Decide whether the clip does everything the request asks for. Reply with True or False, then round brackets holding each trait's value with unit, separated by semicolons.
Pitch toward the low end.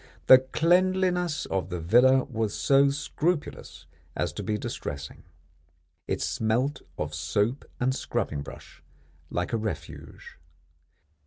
True (125 Hz)